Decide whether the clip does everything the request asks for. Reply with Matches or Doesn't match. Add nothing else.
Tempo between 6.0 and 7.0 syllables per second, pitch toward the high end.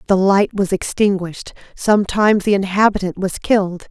Doesn't match